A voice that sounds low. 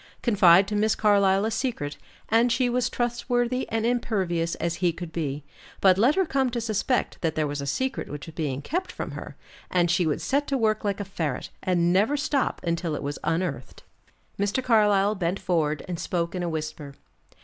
No: high, 190 Hz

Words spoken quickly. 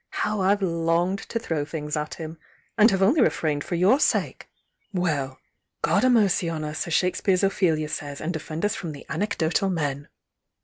No: average, 180 wpm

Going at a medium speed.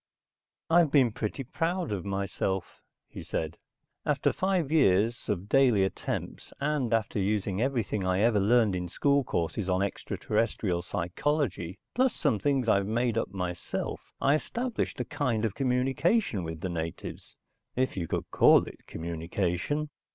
Yes: average, 145 wpm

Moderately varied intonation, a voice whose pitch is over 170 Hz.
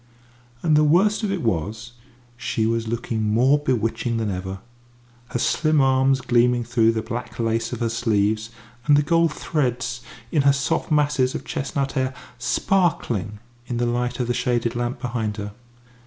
No: average, 3.2 semitones; low, 120 Hz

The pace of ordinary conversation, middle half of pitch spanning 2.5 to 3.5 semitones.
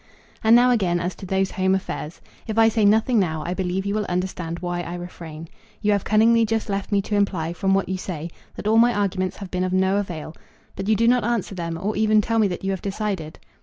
No: fast, 245 wpm; average, 3.2 semitones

